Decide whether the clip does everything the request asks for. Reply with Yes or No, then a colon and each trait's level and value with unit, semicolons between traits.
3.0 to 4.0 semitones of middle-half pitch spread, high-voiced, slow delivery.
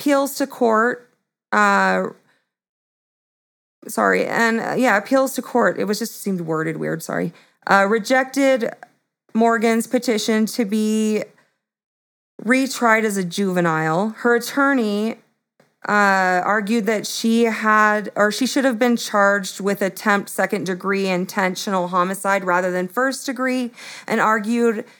Yes: average, 3.6 semitones; high, 220 Hz; slow, 125 wpm